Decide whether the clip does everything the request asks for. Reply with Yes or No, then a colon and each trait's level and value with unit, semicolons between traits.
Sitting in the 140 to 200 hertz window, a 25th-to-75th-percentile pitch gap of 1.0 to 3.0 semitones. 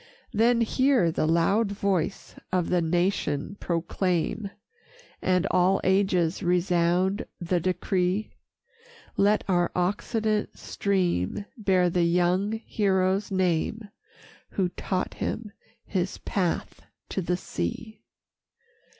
Yes: medium, 185 Hz; narrow, 2.4 semitones